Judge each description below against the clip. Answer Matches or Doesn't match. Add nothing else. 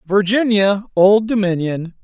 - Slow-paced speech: Matches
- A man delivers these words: Matches